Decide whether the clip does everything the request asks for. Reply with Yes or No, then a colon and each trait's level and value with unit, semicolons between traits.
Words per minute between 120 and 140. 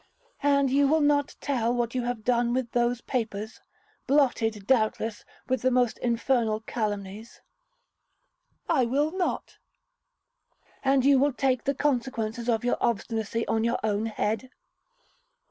Yes: slow, 135 wpm